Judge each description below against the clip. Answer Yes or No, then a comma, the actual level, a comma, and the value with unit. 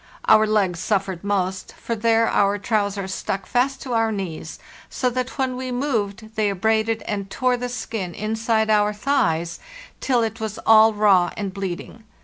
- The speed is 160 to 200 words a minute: Yes, average, 165 wpm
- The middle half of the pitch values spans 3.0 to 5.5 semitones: No, narrow, 2.6 semitones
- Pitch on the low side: No, high, 215 Hz